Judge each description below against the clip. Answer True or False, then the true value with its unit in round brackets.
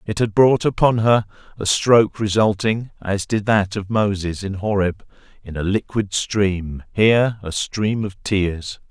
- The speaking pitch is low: True (105 Hz)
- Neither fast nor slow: True (155 wpm)